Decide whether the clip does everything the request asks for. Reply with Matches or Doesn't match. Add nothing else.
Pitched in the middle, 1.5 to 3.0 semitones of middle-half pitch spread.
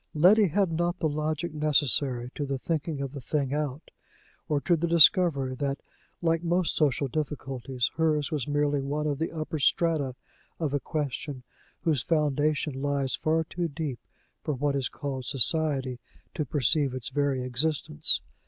Matches